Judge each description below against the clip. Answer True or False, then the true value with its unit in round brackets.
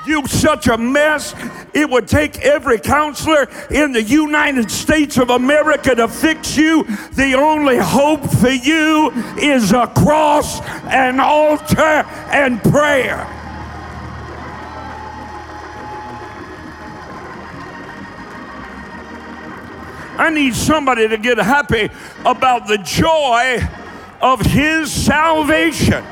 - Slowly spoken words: True (95 wpm)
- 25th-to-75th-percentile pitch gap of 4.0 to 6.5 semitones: False (3.6 semitones)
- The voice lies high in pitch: True (290 Hz)